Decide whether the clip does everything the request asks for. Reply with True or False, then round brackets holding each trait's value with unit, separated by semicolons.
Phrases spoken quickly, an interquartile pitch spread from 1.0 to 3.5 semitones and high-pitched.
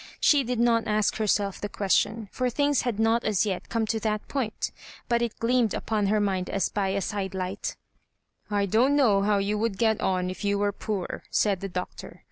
True (215 wpm; 2.5 semitones; 210 Hz)